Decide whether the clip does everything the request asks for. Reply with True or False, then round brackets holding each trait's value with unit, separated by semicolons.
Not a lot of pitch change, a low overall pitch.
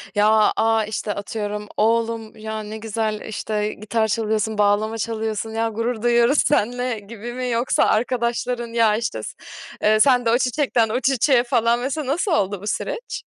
False (2.0 semitones; 225 Hz)